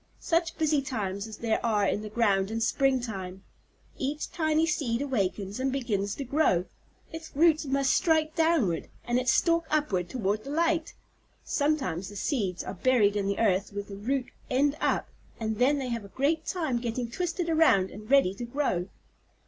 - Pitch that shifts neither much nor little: No, wide, 6.7 semitones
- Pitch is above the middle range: Yes, very high, 250 Hz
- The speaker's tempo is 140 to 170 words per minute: No, average, 180 wpm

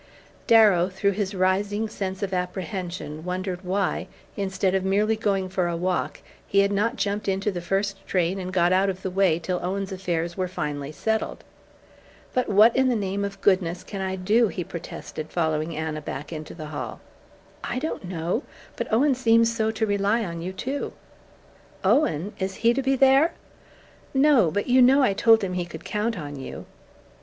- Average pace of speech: Yes, average, 185 wpm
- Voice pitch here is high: Yes, high, 195 Hz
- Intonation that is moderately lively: Yes, average, 3.4 semitones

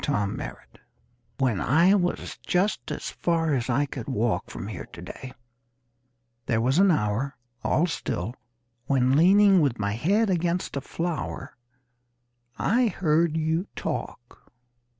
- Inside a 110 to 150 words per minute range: Yes, slow, 135 wpm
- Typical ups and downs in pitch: No, wide, 5.9 semitones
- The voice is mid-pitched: Yes, medium, 155 Hz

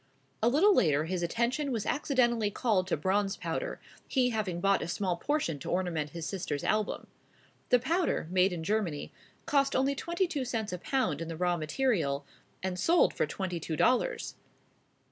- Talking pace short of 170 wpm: No, average, 175 wpm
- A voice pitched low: No, high, 200 Hz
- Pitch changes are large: Yes, wide, 7.1 semitones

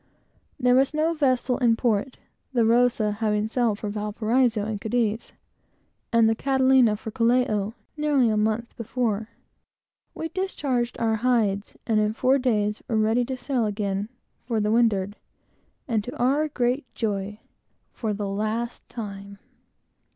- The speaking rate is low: No, average, 145 wpm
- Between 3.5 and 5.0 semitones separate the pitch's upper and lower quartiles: No, average, 3.0 semitones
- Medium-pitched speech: No, high, 230 Hz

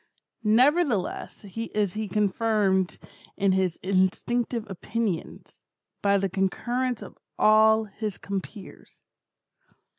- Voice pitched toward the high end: Yes, high, 210 Hz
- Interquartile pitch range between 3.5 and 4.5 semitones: No, average, 3.0 semitones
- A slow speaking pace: Yes, slow, 90 wpm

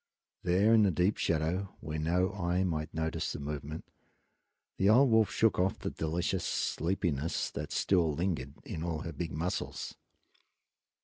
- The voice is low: Yes, very low, 85 Hz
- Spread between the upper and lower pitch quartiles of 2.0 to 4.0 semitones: Yes, average, 3.3 semitones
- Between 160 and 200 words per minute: No, average, 150 wpm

